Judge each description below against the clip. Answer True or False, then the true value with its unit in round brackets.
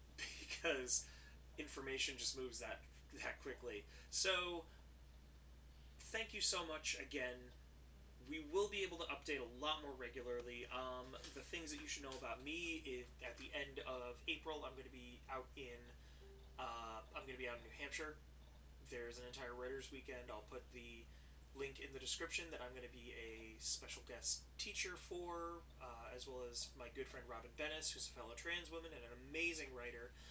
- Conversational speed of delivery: True (185 wpm)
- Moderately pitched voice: False (125 Hz)